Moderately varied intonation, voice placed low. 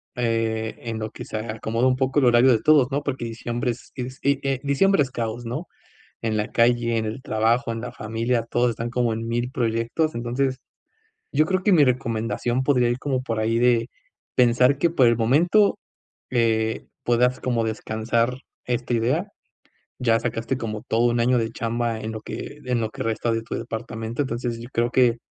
No: narrow, 2.0 semitones; low, 120 Hz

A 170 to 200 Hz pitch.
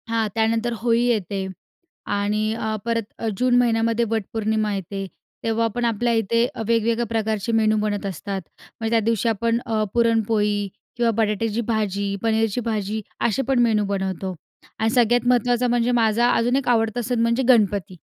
No: high, 225 Hz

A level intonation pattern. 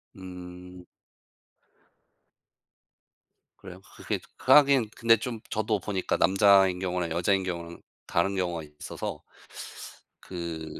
Yes: narrow, 2.3 semitones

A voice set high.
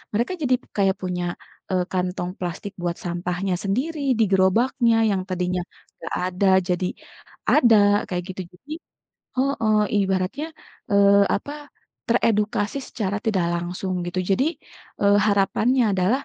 Yes: high, 200 Hz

